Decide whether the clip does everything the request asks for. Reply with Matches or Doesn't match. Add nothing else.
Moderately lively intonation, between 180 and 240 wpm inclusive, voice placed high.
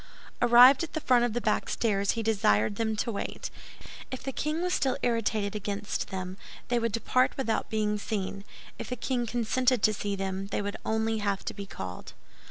Matches